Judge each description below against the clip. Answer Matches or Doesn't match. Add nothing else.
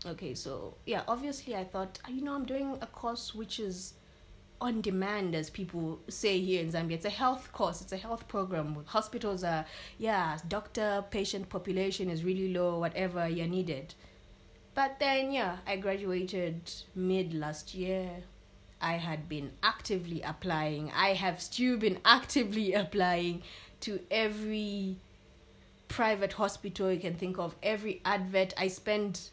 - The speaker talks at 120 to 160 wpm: Matches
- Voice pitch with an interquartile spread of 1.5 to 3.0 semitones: Doesn't match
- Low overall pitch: Doesn't match